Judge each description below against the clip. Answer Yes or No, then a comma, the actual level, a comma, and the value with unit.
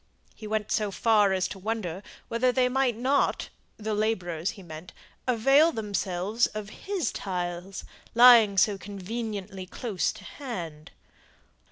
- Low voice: No, high, 210 Hz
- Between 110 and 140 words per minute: Yes, slow, 135 wpm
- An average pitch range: Yes, average, 4.0 semitones